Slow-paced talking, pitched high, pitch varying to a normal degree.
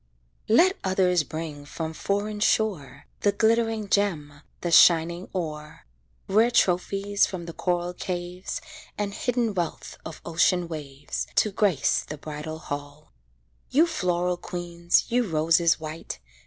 No: slow, 130 wpm; medium, 175 Hz; average, 4.3 semitones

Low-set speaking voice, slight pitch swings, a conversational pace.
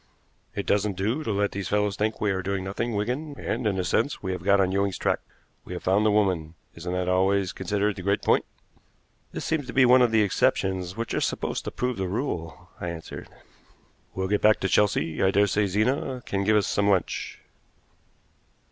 No: low, 100 Hz; narrow, 2.3 semitones; fast, 210 wpm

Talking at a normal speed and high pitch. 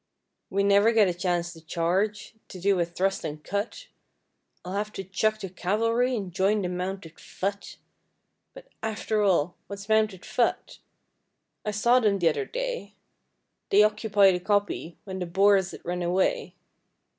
Yes: average, 155 wpm; high, 200 Hz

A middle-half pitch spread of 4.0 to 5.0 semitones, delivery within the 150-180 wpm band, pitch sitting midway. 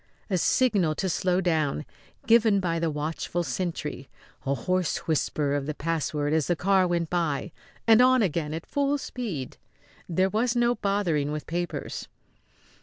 Yes: average, 4.5 semitones; average, 155 wpm; medium, 175 Hz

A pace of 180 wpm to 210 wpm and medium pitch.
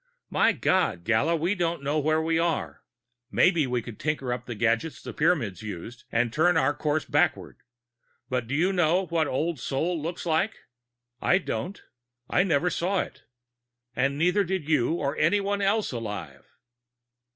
No: average, 160 wpm; medium, 155 Hz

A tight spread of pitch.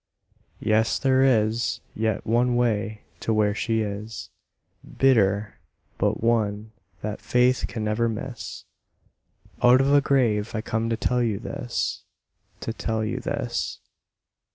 Yes: narrow, 2.3 semitones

